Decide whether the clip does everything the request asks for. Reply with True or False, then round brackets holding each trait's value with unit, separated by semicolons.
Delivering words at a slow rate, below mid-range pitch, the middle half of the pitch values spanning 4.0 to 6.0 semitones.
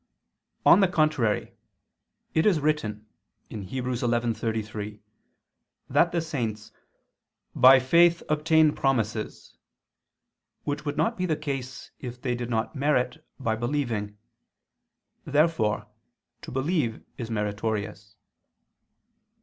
True (100 wpm; 125 Hz; 5.5 semitones)